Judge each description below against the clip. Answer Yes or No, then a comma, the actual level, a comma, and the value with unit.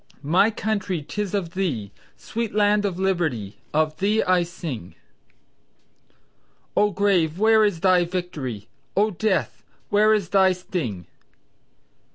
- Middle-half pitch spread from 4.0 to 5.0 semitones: Yes, average, 4.4 semitones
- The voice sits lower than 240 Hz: Yes, medium, 185 Hz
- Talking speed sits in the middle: No, slow, 125 wpm